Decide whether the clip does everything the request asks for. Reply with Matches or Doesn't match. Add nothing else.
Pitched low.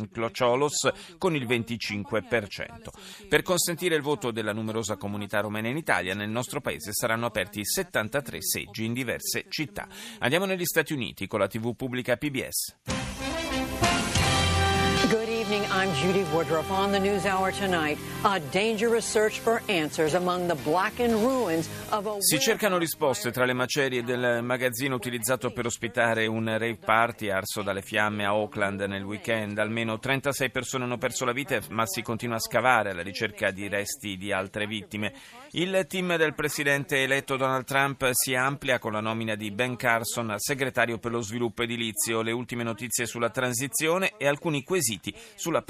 Matches